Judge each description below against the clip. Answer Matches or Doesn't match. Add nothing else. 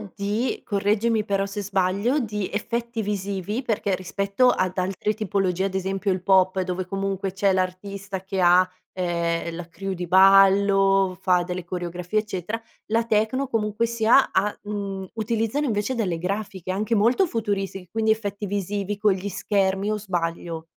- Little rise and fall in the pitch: Matches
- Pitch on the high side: Matches